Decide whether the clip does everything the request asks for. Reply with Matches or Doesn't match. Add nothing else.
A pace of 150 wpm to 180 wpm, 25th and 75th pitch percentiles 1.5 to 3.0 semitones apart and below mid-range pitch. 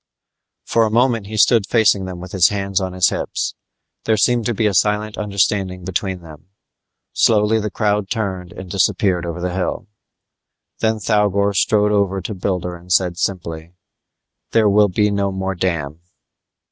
Matches